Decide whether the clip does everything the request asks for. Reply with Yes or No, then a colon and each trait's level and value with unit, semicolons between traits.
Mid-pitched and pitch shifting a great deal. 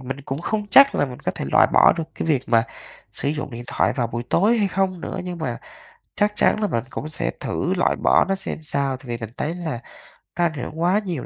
Yes: medium, 155 Hz; wide, 6.5 semitones